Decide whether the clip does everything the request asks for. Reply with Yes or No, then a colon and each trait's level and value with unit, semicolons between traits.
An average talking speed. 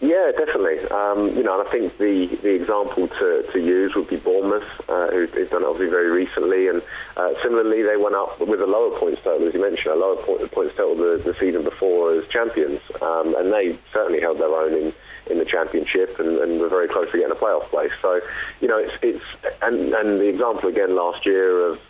No: fast, 225 wpm